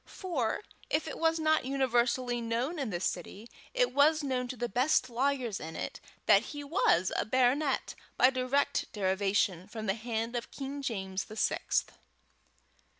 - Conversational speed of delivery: Yes, average, 160 wpm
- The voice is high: Yes, high, 245 Hz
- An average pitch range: Yes, average, 4.6 semitones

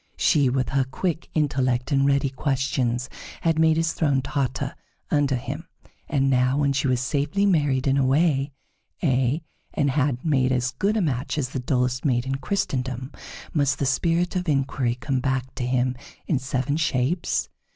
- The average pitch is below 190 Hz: Yes, low, 135 Hz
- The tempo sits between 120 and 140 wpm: No, average, 170 wpm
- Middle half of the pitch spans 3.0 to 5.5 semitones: No, narrow, 2.5 semitones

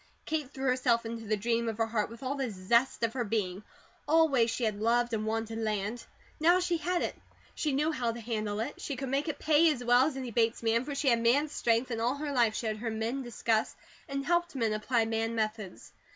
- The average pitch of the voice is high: Yes, high, 235 Hz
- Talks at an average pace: No, fast, 240 wpm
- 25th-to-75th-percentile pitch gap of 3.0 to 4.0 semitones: Yes, average, 3.4 semitones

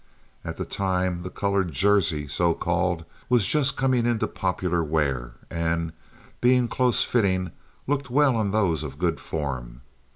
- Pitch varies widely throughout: Yes, wide, 6.0 semitones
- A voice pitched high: No, very low, 90 Hz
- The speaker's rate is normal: Yes, average, 150 wpm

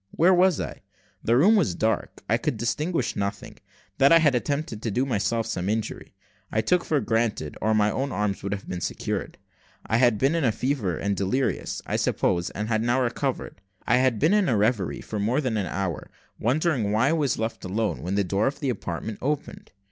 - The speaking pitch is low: Yes, low, 115 Hz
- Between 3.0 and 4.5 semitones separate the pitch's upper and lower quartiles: No, average, 5.1 semitones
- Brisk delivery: Yes, fast, 210 wpm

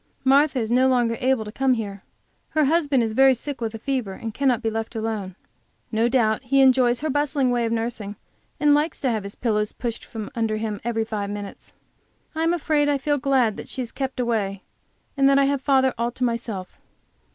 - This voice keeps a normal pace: No, fast, 215 wpm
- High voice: Yes, high, 240 Hz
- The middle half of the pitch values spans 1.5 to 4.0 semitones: Yes, average, 3.6 semitones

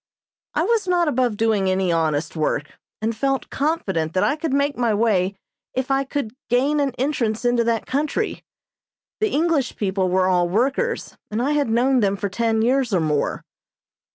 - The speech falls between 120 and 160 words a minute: No, average, 180 wpm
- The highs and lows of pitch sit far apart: Yes, wide, 6.3 semitones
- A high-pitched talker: Yes, high, 235 Hz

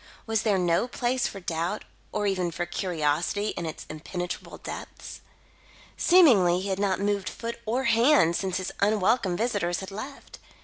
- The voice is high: Yes, high, 195 Hz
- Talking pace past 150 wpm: Yes, average, 160 wpm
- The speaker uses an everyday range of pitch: Yes, average, 4.1 semitones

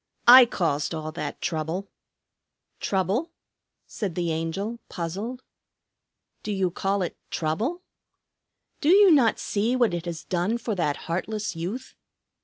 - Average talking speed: No, slow, 130 wpm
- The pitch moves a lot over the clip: Yes, wide, 5.9 semitones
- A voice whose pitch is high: Yes, high, 195 Hz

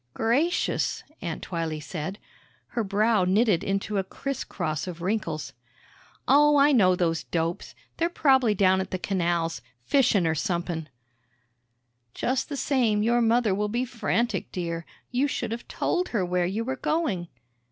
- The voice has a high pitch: Yes, high, 200 Hz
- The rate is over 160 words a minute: No, average, 150 wpm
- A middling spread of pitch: No, wide, 5.8 semitones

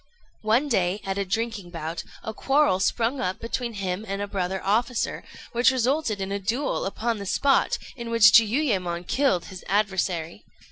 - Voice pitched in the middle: No, high, 210 Hz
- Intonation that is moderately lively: Yes, average, 3.9 semitones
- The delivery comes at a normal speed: Yes, average, 170 wpm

